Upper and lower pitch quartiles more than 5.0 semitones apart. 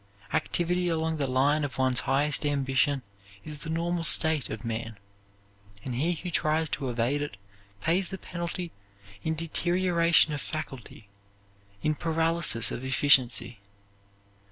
No: average, 4.1 semitones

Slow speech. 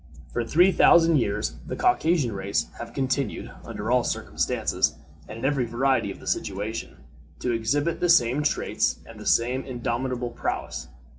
No: average, 150 wpm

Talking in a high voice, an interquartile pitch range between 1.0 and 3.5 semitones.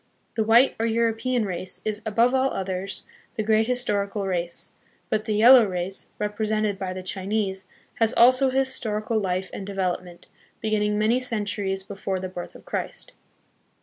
Yes: high, 210 Hz; average, 2.9 semitones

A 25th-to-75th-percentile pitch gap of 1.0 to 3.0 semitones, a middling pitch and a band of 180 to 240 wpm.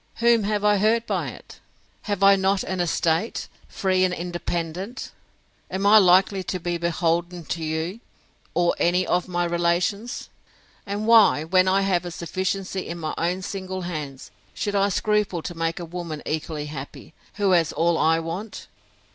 No: average, 2.7 semitones; medium, 180 Hz; average, 160 wpm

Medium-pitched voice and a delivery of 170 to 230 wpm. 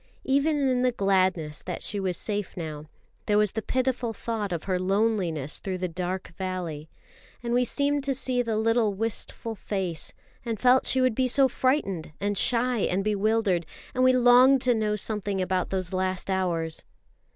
No: high, 210 Hz; average, 175 wpm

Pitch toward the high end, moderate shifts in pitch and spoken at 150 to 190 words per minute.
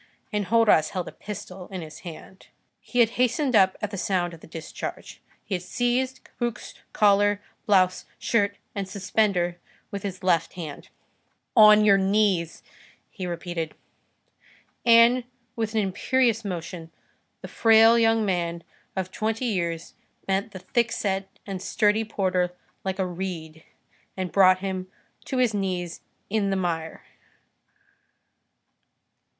No: high, 195 Hz; average, 3.4 semitones; slow, 135 wpm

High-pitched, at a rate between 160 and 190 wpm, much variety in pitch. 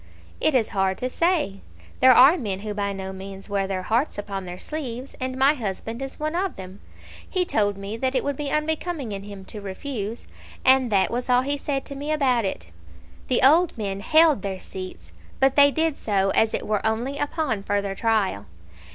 No: high, 230 Hz; fast, 205 wpm; wide, 6.1 semitones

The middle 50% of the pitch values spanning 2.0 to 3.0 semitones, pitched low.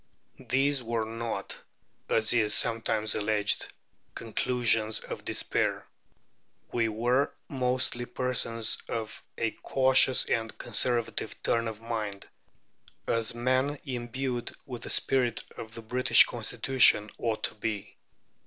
Yes: narrow, 2.4 semitones; low, 115 Hz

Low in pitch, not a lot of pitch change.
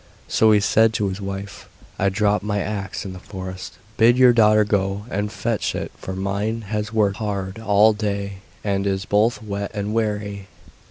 Yes: low, 105 Hz; narrow, 1.6 semitones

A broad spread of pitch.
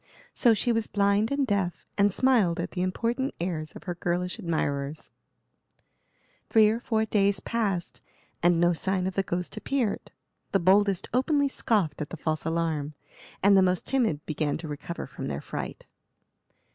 No: average, 4.6 semitones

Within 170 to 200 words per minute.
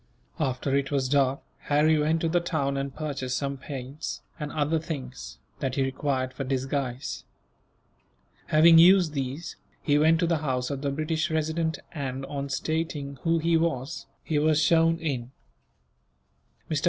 No: average, 155 wpm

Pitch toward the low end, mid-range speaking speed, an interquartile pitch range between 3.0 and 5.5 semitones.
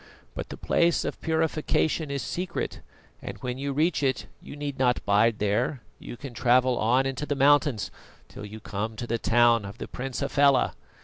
Yes: low, 130 Hz; average, 185 wpm; average, 3.7 semitones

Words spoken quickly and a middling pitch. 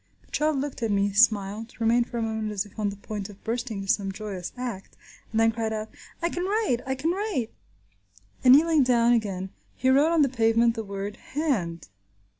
No: fast, 210 wpm; high, 225 Hz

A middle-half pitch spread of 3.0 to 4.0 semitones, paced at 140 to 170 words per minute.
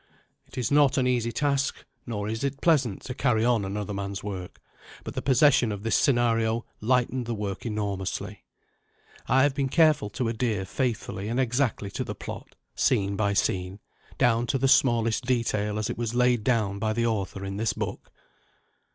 No: average, 3.5 semitones; average, 180 wpm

